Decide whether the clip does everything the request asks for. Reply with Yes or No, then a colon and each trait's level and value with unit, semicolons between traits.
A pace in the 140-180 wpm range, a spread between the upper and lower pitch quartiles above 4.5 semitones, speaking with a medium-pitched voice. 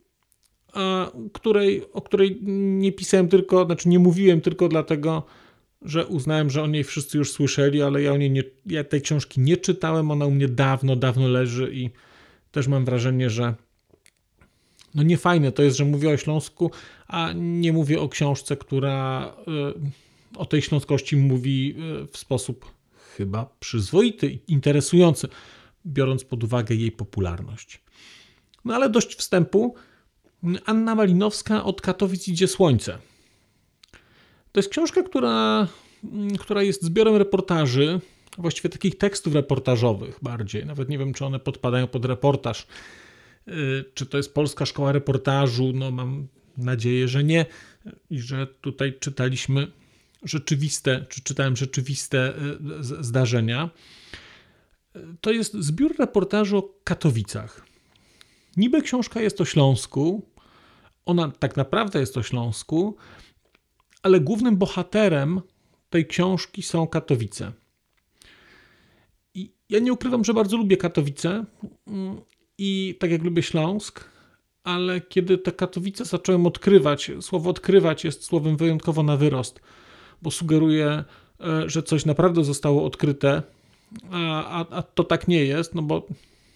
No: average, 130 wpm; wide, 5.4 semitones; medium, 155 Hz